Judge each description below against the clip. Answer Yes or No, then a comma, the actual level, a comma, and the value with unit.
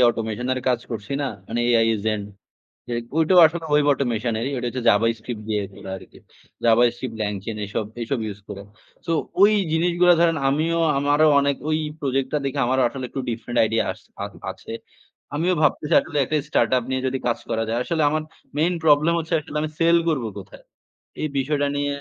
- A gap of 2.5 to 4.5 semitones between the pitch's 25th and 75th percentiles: No, average, 5.1 semitones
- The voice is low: Yes, low, 130 Hz